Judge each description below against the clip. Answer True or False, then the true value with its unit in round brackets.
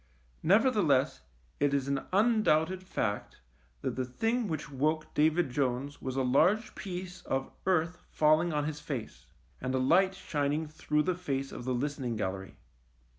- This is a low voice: False (150 Hz)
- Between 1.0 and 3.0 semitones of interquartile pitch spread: False (5.1 semitones)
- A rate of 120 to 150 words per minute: False (160 wpm)